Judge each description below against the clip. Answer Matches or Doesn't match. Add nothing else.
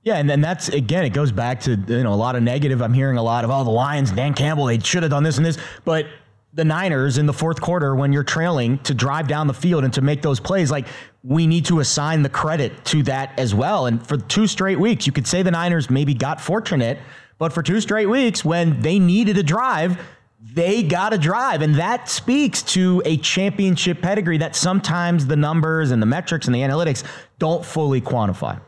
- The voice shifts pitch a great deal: Doesn't match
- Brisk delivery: Matches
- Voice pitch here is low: Doesn't match